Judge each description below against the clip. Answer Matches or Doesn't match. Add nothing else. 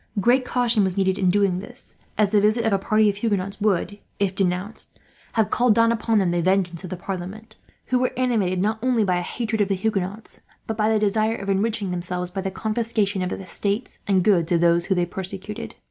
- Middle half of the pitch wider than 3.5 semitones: Doesn't match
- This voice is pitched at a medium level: Doesn't match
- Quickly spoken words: Matches